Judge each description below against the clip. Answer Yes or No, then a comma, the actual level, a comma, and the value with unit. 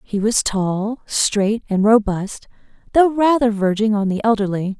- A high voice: Yes, high, 215 Hz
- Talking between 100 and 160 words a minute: Yes, average, 150 wpm